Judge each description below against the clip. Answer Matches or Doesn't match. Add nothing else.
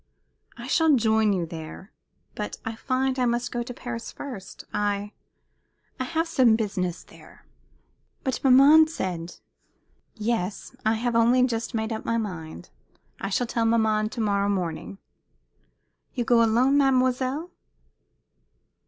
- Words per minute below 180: Matches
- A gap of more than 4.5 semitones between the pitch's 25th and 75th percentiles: Doesn't match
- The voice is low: Doesn't match